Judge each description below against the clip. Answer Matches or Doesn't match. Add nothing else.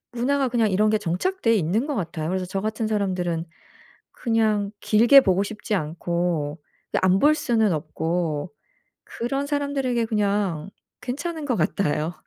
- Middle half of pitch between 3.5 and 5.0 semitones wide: Doesn't match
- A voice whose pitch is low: Doesn't match